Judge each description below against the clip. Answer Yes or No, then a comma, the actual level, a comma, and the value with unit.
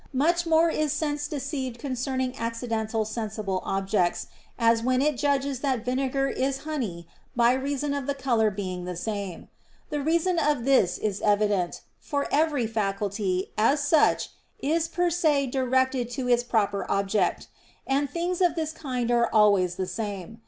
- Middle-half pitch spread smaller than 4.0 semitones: No, average, 5.2 semitones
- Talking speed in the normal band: Yes, average, 155 wpm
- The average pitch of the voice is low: No, very high, 250 Hz